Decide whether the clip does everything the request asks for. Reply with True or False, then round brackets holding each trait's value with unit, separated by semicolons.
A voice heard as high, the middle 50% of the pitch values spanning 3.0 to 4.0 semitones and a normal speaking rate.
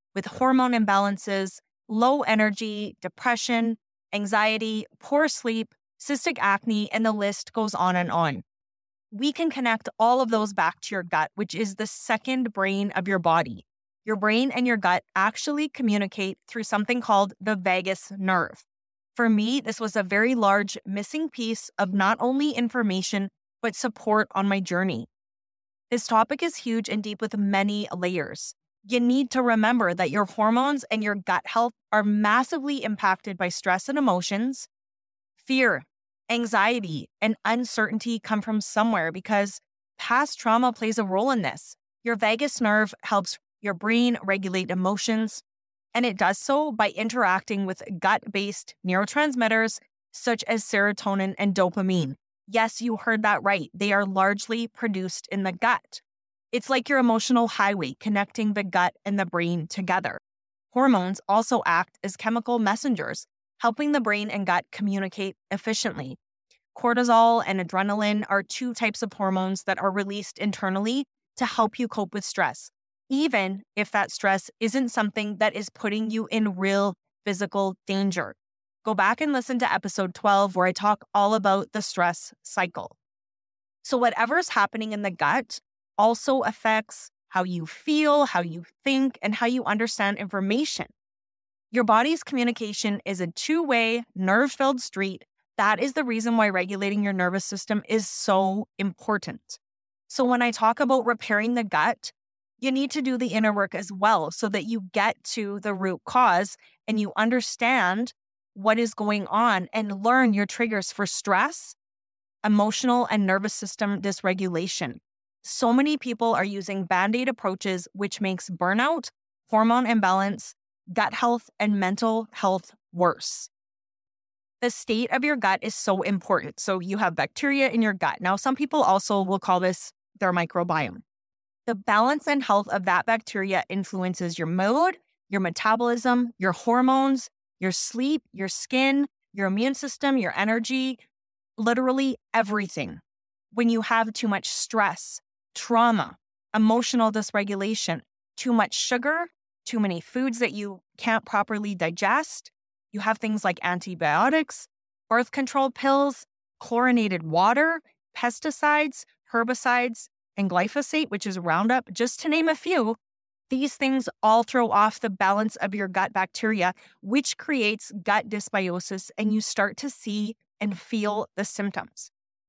True (215 Hz; 3.6 semitones; 150 wpm)